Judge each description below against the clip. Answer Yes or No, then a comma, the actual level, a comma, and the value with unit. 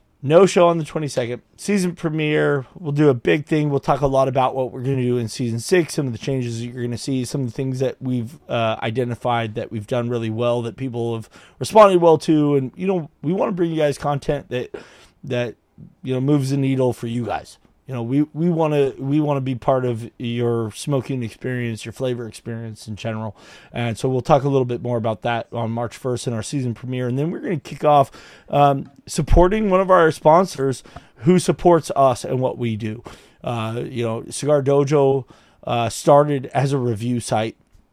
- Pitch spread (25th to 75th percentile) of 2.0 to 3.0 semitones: No, average, 3.8 semitones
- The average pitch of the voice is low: Yes, low, 130 Hz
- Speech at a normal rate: No, fast, 220 wpm